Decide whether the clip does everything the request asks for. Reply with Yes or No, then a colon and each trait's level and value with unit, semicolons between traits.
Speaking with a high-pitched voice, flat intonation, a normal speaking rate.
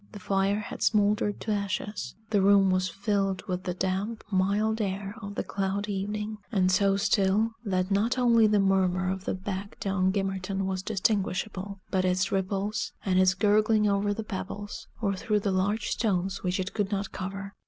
Yes: high, 195 Hz; narrow, 1.6 semitones; average, 180 wpm